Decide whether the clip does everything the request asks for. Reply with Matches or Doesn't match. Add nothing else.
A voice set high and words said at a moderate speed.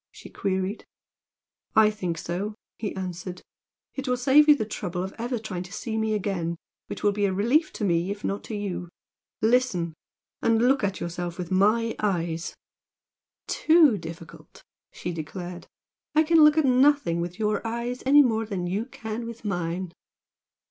Matches